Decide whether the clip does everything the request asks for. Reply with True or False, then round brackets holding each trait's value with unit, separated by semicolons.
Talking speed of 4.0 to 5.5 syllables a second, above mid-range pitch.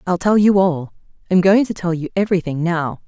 False (5.0 syllables/s; 180 Hz)